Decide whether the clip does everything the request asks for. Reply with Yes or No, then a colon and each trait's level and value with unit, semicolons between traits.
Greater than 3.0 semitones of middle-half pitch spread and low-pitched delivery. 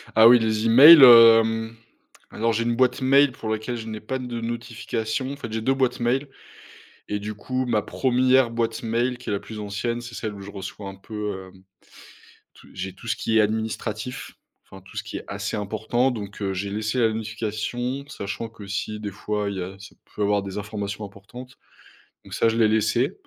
No: average, 2.7 semitones; low, 110 Hz